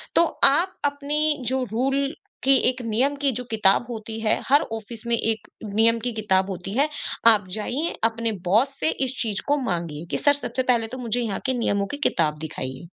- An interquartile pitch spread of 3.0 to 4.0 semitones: No, average, 4.5 semitones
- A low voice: No, high, 230 Hz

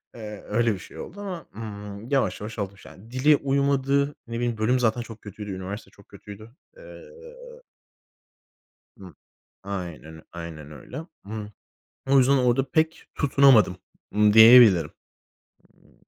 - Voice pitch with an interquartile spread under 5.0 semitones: No, wide, 5.4 semitones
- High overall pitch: No, low, 115 Hz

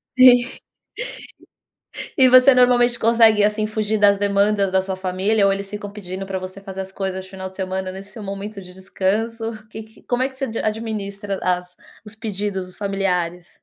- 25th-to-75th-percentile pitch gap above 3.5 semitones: No, narrow, 2.5 semitones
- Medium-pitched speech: No, high, 200 Hz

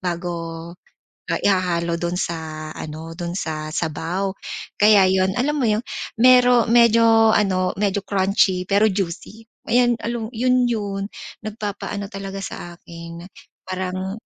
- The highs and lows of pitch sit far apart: No, average, 4.2 semitones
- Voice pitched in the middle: No, high, 195 Hz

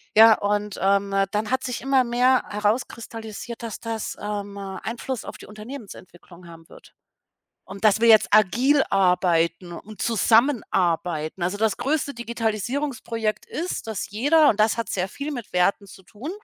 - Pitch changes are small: No, average, 3.4 semitones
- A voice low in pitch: No, high, 215 Hz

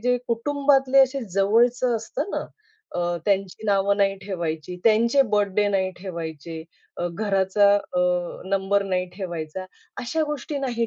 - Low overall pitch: No, high, 200 Hz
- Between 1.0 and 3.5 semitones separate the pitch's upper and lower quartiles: No, average, 4.4 semitones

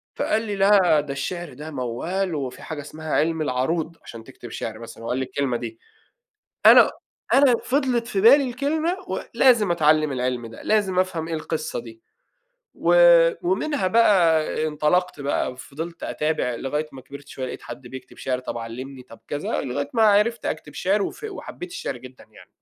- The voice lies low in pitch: No, medium, 155 Hz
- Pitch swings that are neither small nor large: No, wide, 7.4 semitones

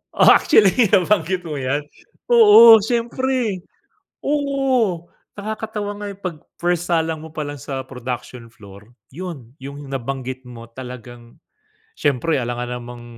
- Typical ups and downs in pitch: No, wide, 8.5 semitones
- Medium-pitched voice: Yes, medium, 155 Hz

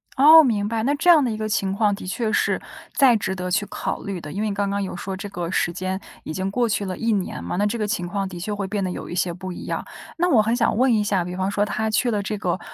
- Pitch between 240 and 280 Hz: No, high, 205 Hz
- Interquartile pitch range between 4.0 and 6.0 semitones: No, average, 2.8 semitones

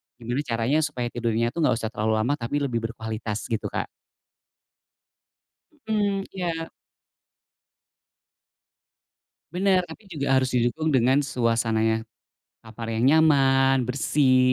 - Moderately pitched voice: No, low, 125 Hz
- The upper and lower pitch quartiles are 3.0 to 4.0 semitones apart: No, average, 4.4 semitones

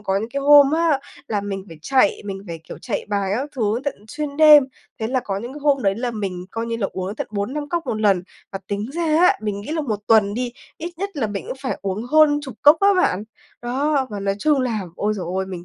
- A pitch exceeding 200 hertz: Yes, high, 230 Hz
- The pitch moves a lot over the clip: Yes, wide, 6.3 semitones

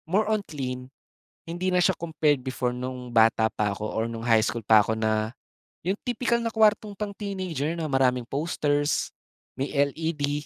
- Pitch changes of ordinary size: No, wide, 6.8 semitones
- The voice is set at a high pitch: No, medium, 145 Hz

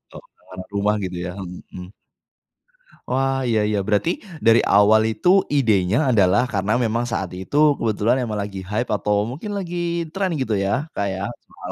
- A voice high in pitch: No, low, 105 Hz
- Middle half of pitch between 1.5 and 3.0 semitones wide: No, average, 4.2 semitones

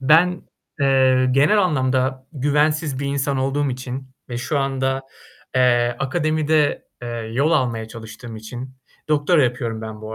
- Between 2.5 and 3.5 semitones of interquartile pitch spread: Yes, average, 2.8 semitones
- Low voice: Yes, low, 130 Hz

